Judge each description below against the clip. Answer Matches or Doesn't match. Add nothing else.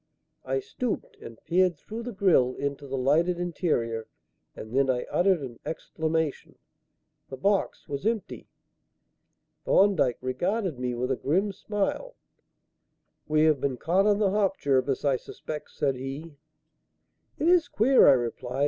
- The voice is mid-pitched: Matches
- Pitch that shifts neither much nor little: Doesn't match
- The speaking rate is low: Doesn't match